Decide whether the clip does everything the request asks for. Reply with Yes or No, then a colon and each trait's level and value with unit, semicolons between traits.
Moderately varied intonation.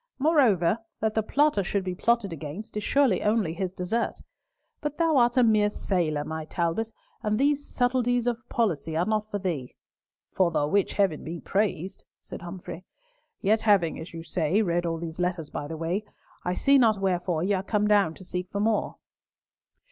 Yes: average, 4.6 semitones